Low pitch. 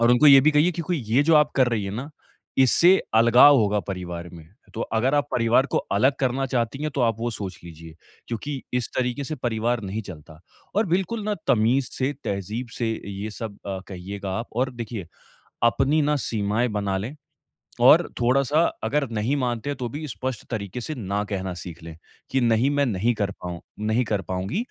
Yes: low, 120 Hz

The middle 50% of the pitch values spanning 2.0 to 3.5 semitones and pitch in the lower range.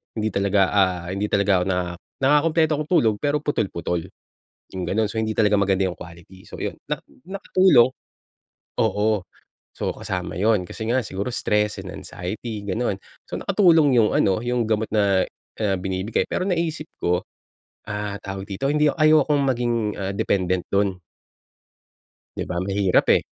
No: average, 4.6 semitones; low, 105 Hz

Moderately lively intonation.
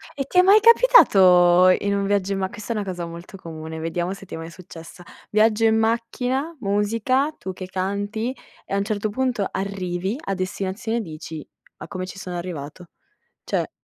Yes: average, 3.8 semitones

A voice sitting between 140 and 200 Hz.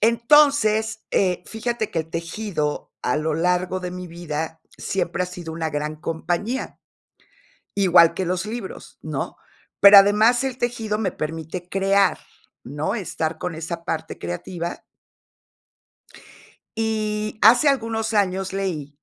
Yes: medium, 185 Hz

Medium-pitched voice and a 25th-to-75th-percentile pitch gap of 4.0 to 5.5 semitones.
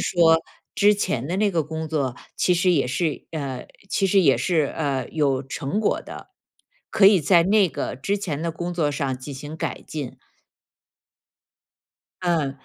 Yes: medium, 160 Hz; average, 4.4 semitones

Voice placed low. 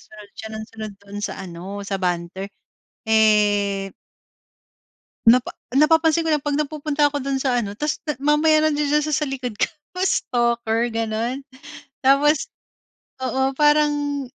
No: very high, 260 Hz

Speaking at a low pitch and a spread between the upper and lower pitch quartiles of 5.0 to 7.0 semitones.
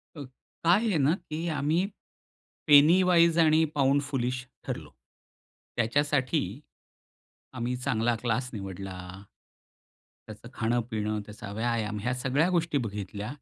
Yes: low, 125 Hz; wide, 5.5 semitones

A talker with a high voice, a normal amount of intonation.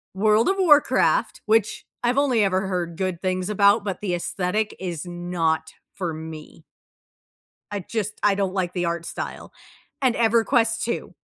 Yes: high, 195 Hz; average, 4.1 semitones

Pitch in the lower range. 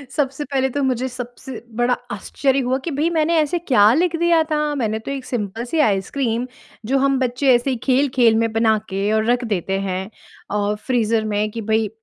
No: very high, 250 Hz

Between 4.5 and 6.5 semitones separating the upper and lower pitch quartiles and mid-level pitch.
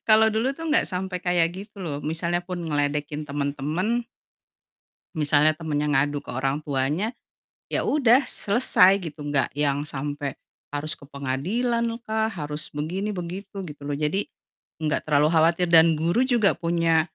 Yes: average, 5.1 semitones; medium, 165 Hz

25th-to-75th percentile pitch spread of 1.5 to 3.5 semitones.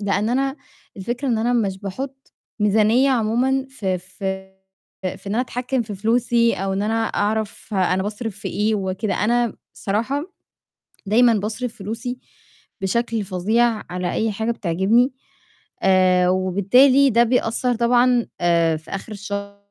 No: average, 3.9 semitones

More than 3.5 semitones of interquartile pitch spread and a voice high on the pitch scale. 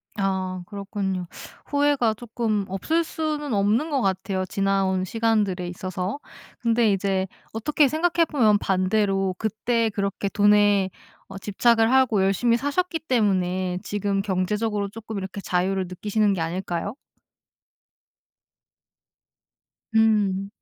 No: average, 3.2 semitones; high, 205 Hz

